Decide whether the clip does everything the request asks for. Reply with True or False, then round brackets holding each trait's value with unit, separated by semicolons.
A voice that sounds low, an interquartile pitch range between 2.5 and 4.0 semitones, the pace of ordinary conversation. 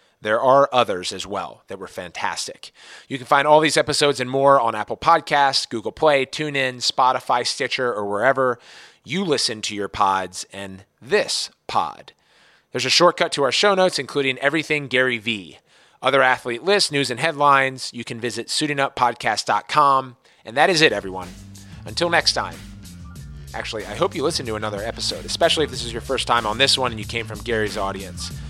False (125 Hz; 5.2 semitones; 185 wpm)